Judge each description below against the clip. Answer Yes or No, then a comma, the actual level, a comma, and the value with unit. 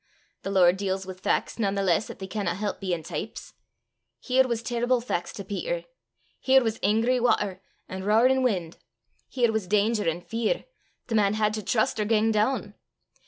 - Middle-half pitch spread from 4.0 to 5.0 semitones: No, average, 3.4 semitones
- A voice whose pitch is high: Yes, high, 210 Hz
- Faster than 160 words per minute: Yes, average, 180 wpm